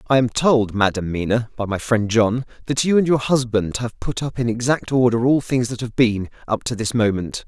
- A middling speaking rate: No, fast, 235 wpm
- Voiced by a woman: No, male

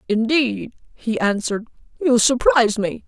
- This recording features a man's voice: No, female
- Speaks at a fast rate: No, slow, 115 wpm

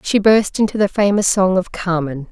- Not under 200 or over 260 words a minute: Yes, fast, 205 wpm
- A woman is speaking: Yes, female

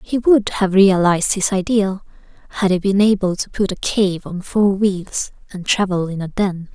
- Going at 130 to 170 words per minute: No, average, 195 wpm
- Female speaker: Yes, female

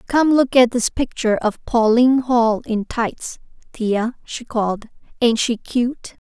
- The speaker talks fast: No, average, 155 wpm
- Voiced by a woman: Yes, female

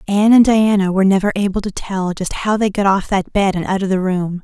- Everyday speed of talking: No, fast, 270 wpm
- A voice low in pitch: No, high, 195 Hz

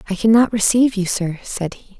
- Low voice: No, high, 205 Hz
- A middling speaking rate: No, fast, 210 wpm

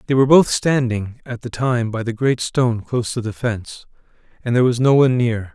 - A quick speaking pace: Yes, fast, 225 wpm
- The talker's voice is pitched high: No, low, 120 Hz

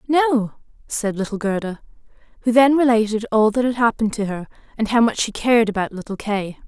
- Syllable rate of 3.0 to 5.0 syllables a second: No, 5.7 syllables/s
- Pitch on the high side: Yes, high, 225 Hz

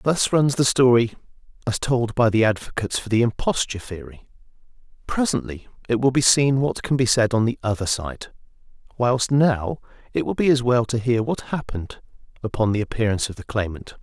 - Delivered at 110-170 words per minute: No, average, 185 wpm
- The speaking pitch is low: Yes, low, 120 Hz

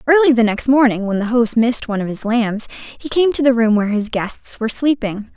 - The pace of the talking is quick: Yes, fast, 245 wpm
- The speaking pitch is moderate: No, high, 235 Hz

